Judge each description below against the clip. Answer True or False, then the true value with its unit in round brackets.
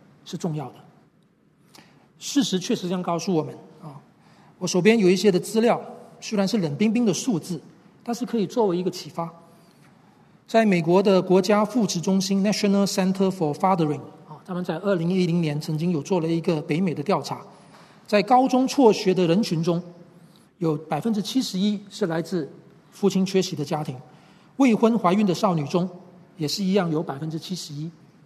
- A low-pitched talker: False (185 Hz)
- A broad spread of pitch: False (3.6 semitones)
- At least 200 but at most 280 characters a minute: False (310 characters per minute)